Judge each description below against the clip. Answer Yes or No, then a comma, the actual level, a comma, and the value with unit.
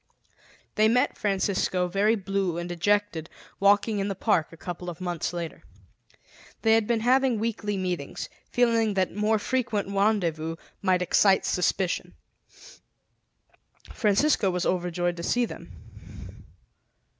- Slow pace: Yes, slow, 125 wpm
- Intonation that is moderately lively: Yes, average, 3.5 semitones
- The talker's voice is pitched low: No, high, 195 Hz